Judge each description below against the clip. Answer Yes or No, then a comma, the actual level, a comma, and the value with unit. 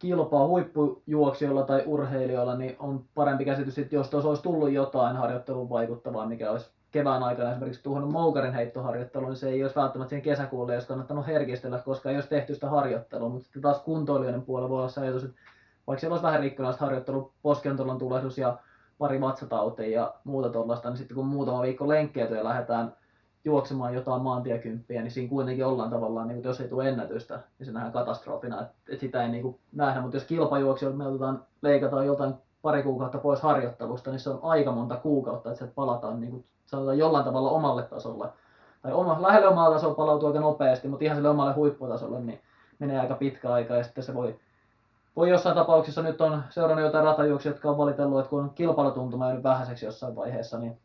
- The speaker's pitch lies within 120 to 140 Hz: Yes, low, 135 Hz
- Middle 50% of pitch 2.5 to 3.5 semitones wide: Yes, average, 2.8 semitones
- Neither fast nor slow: No, fast, 190 wpm